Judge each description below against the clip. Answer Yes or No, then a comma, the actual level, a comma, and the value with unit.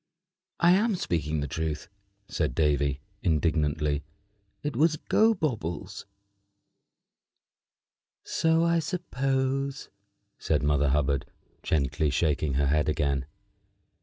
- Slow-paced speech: Yes, slow, 95 wpm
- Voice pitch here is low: Yes, very low, 80 Hz